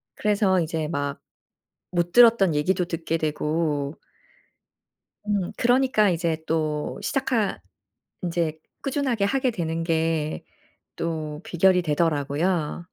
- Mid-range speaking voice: Yes, medium, 170 Hz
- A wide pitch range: No, average, 4.1 semitones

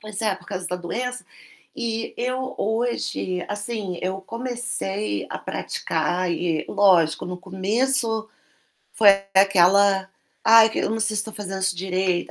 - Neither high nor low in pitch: No, high, 200 Hz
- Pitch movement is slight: No, average, 3.4 semitones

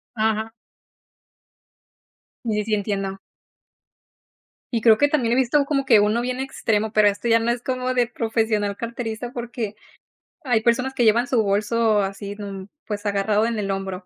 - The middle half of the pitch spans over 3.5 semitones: No, narrow, 2.6 semitones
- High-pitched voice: Yes, high, 225 Hz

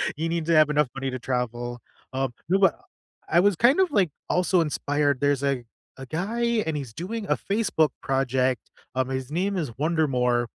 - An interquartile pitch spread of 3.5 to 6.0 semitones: Yes, average, 5.3 semitones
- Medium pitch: Yes, medium, 145 Hz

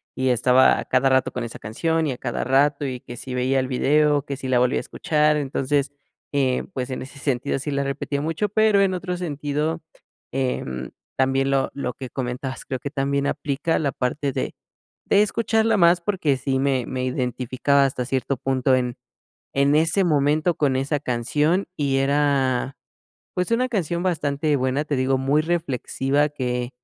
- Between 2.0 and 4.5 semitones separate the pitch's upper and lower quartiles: Yes, average, 2.7 semitones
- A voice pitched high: No, medium, 140 Hz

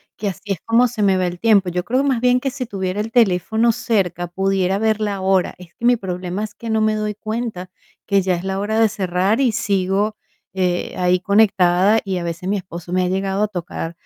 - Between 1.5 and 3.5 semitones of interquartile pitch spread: Yes, average, 3.2 semitones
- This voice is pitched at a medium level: No, high, 195 Hz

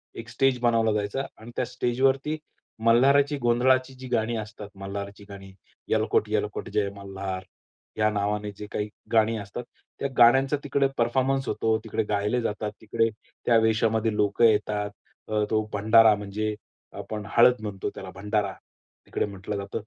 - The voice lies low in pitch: Yes, low, 110 Hz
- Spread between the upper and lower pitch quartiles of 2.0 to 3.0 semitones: Yes, average, 2.7 semitones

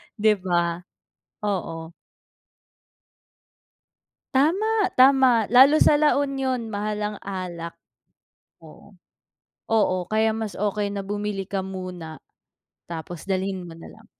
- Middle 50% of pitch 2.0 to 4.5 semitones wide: No, average, 5.0 semitones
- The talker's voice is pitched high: Yes, high, 205 Hz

